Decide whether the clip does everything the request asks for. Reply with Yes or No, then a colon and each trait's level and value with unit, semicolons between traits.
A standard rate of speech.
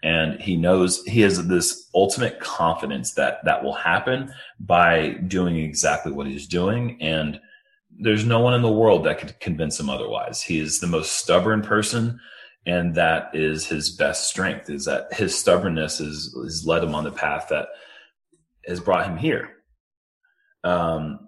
Yes: average, 165 wpm